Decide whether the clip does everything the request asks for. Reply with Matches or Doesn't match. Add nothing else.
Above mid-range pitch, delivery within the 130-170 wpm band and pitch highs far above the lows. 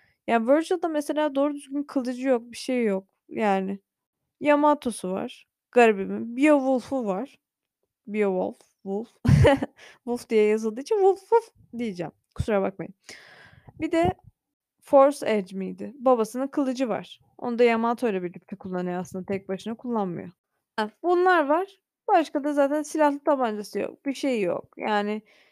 Matches